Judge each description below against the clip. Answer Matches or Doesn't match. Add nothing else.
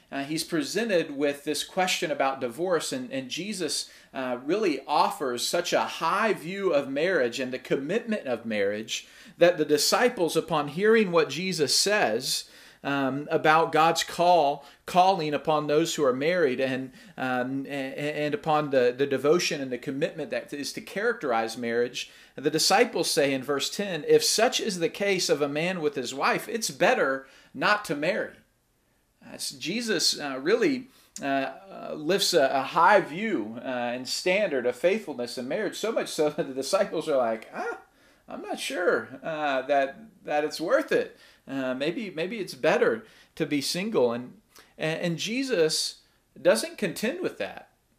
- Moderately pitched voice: Matches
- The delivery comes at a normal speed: Matches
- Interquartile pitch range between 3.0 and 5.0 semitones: Doesn't match